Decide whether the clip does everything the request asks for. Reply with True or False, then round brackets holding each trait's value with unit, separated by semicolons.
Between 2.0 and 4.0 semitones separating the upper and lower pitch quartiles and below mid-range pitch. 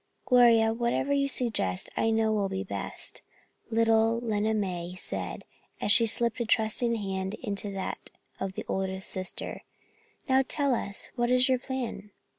False (3.5 semitones; 225 Hz)